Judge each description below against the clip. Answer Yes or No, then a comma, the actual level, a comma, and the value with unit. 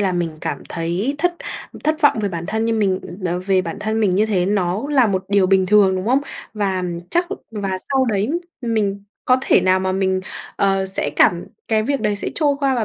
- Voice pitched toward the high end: Yes, high, 200 Hz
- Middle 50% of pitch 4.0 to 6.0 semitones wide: No, average, 3.3 semitones